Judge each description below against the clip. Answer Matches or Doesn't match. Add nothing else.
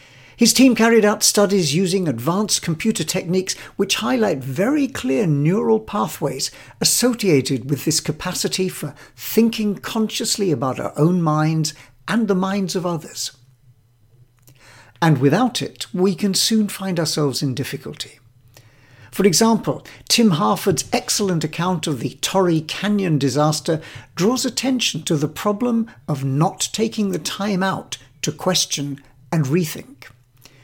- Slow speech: Matches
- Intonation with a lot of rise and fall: Matches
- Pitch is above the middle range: Doesn't match